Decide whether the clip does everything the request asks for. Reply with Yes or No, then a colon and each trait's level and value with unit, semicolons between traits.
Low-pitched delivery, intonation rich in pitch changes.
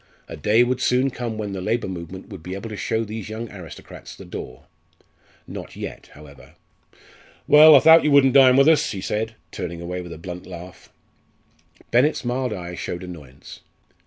Yes: low, 105 Hz; wide, 5.9 semitones